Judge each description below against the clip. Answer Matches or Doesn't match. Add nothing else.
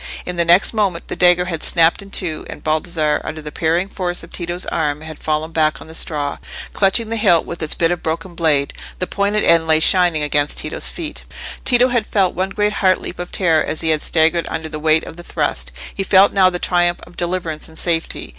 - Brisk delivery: Matches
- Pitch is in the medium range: Matches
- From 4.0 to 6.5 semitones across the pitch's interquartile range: Doesn't match